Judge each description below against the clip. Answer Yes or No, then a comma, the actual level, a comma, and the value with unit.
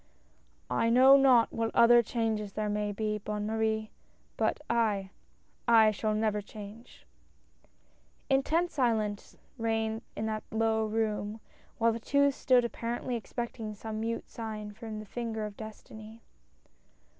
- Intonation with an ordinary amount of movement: No, narrow, 1.6 semitones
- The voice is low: No, high, 220 Hz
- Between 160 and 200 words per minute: No, average, 145 wpm